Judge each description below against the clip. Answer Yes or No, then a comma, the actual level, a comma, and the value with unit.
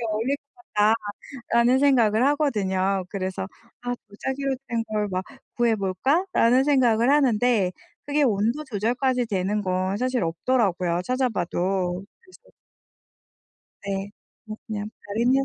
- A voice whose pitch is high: Yes, high, 225 Hz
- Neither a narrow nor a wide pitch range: Yes, average, 5.0 semitones